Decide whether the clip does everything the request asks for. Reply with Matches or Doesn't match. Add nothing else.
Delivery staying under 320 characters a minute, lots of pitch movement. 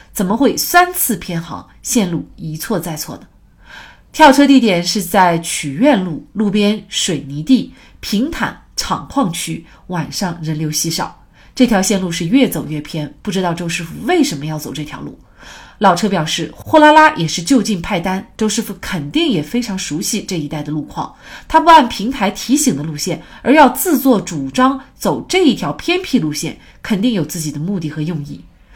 Matches